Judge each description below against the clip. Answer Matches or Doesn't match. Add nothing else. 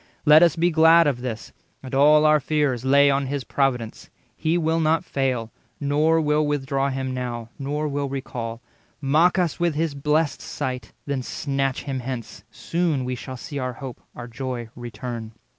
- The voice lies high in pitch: Doesn't match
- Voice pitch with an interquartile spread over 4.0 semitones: Doesn't match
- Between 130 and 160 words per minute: Doesn't match